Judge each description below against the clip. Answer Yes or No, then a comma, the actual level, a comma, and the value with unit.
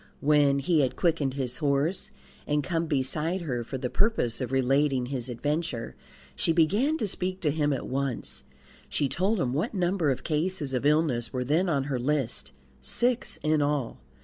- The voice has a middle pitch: Yes, medium, 145 Hz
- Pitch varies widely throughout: No, average, 4.2 semitones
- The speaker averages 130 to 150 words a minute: No, average, 175 wpm